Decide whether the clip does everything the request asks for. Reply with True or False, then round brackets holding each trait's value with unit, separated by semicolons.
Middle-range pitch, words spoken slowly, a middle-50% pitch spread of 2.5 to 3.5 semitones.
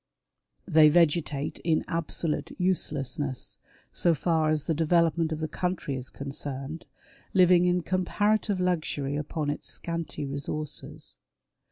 True (160 Hz; 120 wpm; 3.1 semitones)